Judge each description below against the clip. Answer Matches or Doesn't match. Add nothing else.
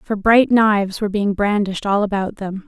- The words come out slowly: Doesn't match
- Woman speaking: Matches